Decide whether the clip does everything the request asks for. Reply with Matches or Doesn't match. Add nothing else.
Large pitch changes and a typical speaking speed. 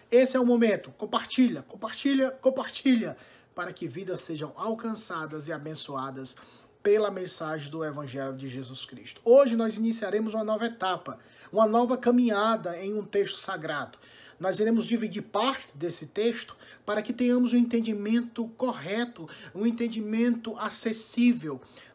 Matches